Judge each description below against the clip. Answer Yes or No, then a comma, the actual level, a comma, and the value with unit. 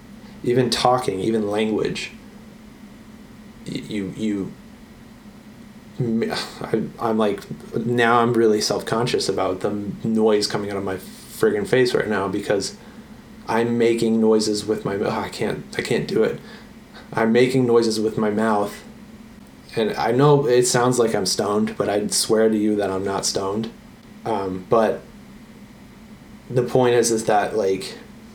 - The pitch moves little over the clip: No, average, 3.3 semitones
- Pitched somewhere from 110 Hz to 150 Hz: Yes, low, 115 Hz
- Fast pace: No, average, 150 wpm